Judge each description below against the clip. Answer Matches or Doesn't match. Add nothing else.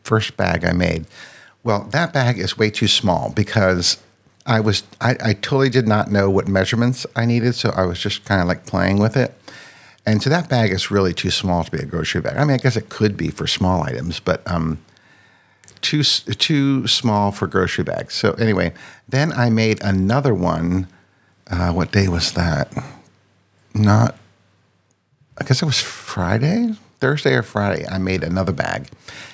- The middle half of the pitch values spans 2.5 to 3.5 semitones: Doesn't match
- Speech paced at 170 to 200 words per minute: Matches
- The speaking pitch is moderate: Doesn't match